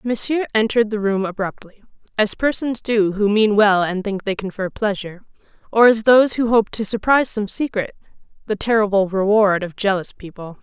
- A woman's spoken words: Yes, female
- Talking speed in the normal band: Yes, average, 175 wpm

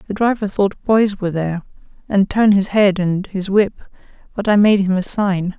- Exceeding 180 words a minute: Yes, fast, 205 wpm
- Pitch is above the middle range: Yes, high, 195 Hz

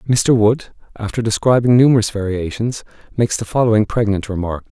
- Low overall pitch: Yes, low, 110 Hz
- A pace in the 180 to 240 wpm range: No, average, 140 wpm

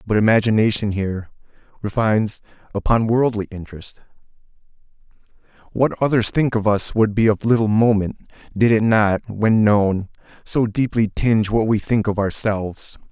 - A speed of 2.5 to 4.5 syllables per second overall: No, 4.9 syllables/s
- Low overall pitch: Yes, low, 110 Hz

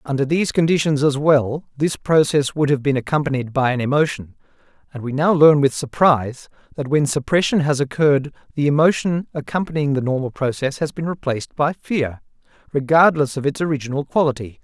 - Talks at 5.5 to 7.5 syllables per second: Yes, 5.7 syllables/s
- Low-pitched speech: No, medium, 145 Hz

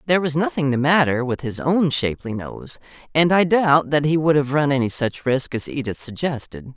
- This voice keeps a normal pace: No, fast, 215 wpm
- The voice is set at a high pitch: No, medium, 140 Hz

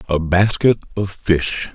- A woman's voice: No, male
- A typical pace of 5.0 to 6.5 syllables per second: No, 3.7 syllables/s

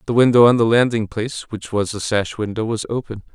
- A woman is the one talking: No, male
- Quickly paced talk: Yes, fast, 235 wpm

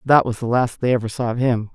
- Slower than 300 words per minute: No, fast, 310 wpm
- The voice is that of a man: No, female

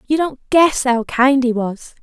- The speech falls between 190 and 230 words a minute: Yes, fast, 205 wpm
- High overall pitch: Yes, very high, 260 Hz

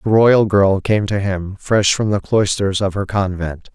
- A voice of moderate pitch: No, low, 100 Hz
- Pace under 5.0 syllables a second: Yes, 4.2 syllables/s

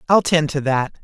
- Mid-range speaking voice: Yes, medium, 150 Hz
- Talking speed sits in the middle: No, fast, 230 wpm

